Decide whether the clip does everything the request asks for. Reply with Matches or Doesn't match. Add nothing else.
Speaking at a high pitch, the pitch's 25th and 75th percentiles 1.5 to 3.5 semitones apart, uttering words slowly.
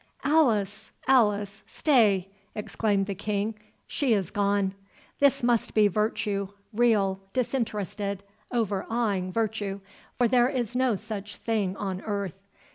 Matches